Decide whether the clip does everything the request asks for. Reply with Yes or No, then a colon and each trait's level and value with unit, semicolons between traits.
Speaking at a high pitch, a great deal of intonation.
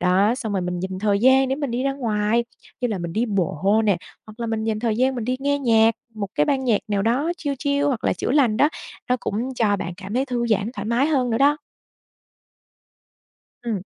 No: high, 230 Hz; average, 4.2 semitones